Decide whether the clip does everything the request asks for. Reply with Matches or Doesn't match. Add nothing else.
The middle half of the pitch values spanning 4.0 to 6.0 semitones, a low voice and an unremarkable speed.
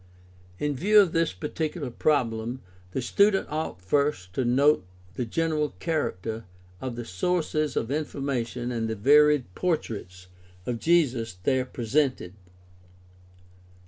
Doesn't match